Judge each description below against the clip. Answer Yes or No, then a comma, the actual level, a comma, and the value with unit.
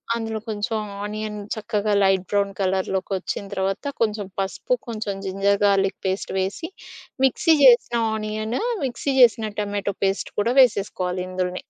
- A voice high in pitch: Yes, high, 205 Hz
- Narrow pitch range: Yes, narrow, 2.3 semitones